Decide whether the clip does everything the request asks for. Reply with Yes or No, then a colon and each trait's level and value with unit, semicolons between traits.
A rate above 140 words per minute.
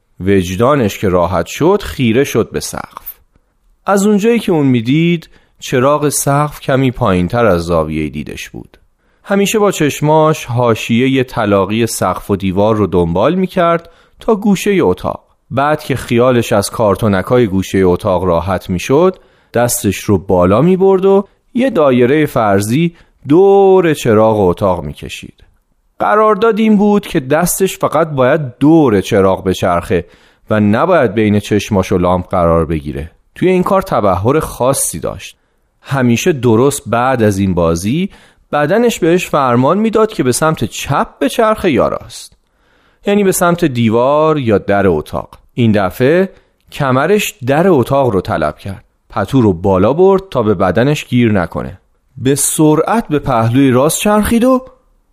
Yes: average, 150 wpm